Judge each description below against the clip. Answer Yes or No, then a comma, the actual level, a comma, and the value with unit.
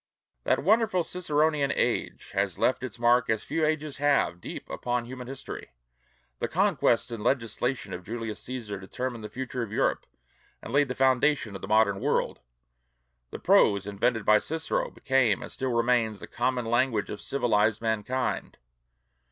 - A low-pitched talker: Yes, low, 120 Hz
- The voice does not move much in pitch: No, average, 3.8 semitones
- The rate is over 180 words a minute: No, average, 160 wpm